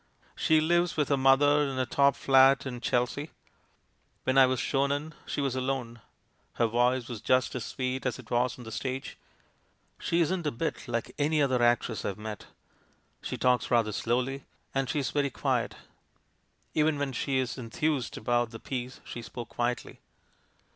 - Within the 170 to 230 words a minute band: Yes, average, 175 wpm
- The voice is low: Yes, low, 130 Hz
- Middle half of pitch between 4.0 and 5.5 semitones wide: No, average, 2.7 semitones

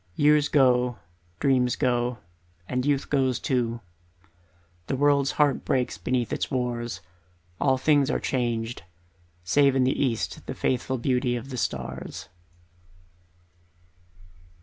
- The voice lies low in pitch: Yes, low, 125 Hz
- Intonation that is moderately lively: No, narrow, 2.2 semitones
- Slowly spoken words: Yes, slow, 120 wpm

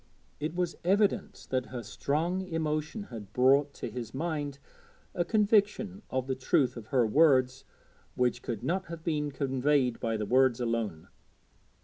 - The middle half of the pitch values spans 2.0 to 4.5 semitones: No, average, 4.9 semitones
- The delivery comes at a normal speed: Yes, average, 150 wpm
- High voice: No, medium, 140 Hz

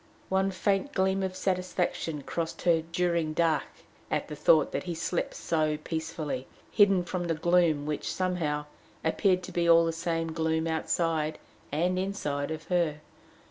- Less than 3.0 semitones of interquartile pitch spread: Yes, narrow, 2.5 semitones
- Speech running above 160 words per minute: No, average, 155 wpm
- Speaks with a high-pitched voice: No, medium, 165 Hz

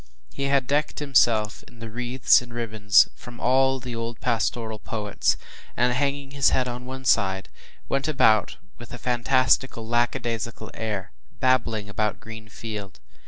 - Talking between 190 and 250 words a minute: No, average, 145 wpm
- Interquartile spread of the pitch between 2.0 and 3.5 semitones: Yes, average, 2.8 semitones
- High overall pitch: No, low, 120 Hz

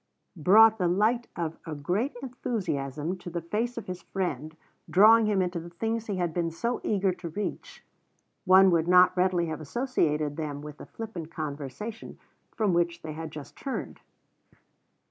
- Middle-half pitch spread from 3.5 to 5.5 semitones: Yes, average, 5.0 semitones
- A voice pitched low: No, medium, 180 Hz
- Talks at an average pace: Yes, average, 165 wpm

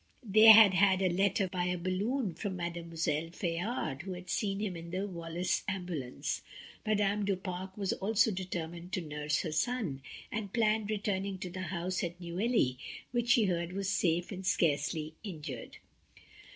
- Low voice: No, medium, 185 Hz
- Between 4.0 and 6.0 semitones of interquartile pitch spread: No, average, 3.0 semitones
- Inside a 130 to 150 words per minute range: No, average, 165 wpm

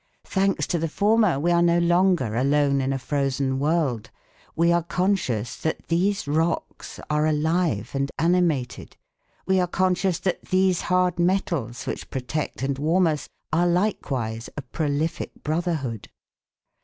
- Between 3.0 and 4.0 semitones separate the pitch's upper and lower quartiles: No, average, 4.5 semitones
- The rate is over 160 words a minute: No, average, 145 wpm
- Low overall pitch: No, medium, 160 Hz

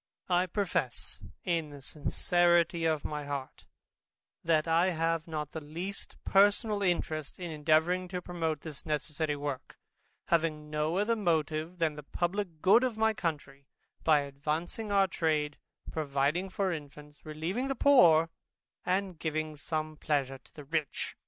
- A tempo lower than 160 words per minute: Yes, average, 145 wpm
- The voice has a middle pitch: Yes, medium, 160 Hz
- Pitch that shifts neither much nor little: Yes, average, 3.1 semitones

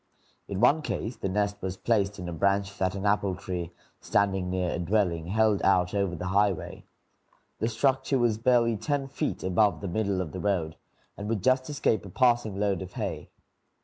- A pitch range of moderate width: Yes, average, 3.0 semitones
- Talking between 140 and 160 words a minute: No, average, 190 wpm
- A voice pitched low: Yes, low, 100 Hz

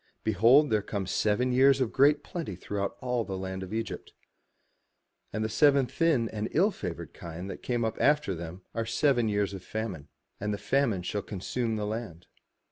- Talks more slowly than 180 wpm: No, average, 185 wpm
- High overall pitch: No, low, 110 Hz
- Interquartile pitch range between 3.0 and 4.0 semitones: No, average, 4.6 semitones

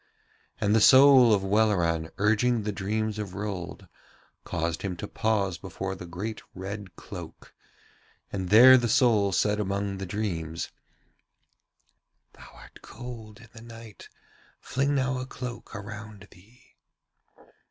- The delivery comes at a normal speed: No, slow, 130 wpm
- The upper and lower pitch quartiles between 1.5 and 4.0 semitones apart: Yes, average, 3.0 semitones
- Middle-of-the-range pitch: No, low, 105 Hz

